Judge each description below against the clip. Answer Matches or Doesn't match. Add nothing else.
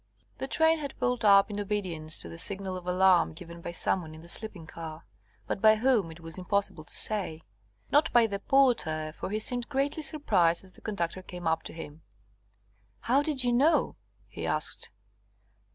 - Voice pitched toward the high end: Matches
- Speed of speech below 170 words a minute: Doesn't match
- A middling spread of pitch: Doesn't match